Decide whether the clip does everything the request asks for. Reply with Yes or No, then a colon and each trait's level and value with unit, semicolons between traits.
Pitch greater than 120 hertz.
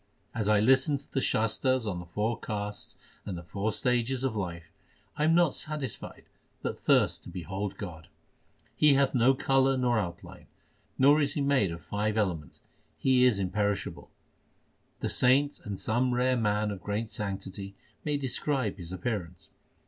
No: low, 110 Hz